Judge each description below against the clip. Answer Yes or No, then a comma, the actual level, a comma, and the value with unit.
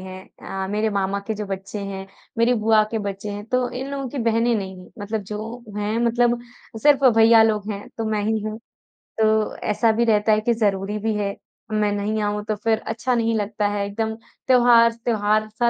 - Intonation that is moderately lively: No, narrow, 1.9 semitones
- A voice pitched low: No, high, 215 Hz